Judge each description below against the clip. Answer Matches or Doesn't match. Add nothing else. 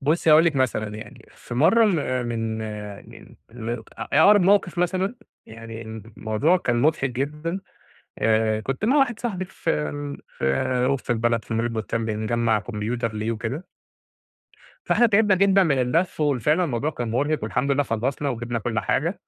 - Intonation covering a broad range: Matches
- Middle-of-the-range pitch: Doesn't match